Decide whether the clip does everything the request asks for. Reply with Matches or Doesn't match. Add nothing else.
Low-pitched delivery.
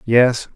Matches